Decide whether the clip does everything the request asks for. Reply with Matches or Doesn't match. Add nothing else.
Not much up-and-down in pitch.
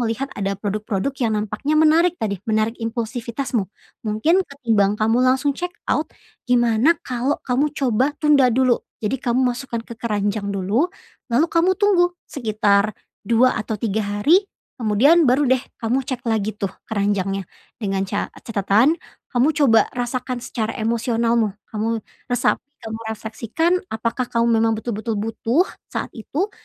Doesn't match